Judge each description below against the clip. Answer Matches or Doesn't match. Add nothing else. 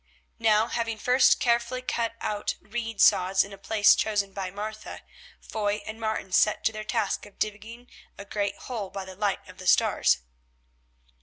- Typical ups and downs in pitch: Doesn't match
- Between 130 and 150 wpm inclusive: Doesn't match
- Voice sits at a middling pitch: Doesn't match